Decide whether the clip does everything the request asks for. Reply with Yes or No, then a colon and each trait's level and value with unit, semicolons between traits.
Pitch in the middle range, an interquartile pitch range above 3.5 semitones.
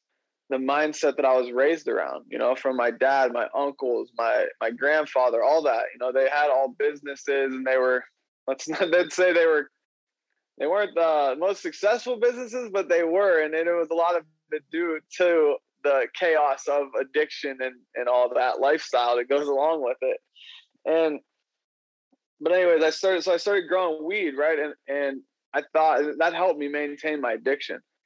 Yes: medium, 155 Hz; average, 5.2 semitones